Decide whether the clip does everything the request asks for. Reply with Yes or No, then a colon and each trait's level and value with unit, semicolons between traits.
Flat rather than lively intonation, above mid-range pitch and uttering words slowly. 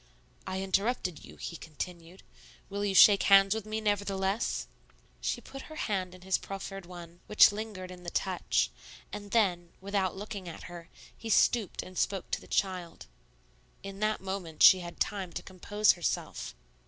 No: narrow, 2.3 semitones; high, 195 Hz; average, 165 wpm